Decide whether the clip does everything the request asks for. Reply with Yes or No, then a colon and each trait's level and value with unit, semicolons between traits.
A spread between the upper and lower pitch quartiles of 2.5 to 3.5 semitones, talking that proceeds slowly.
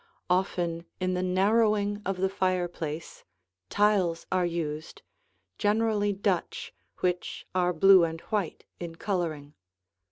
Yes: average, 3.1 semitones; slow, 115 wpm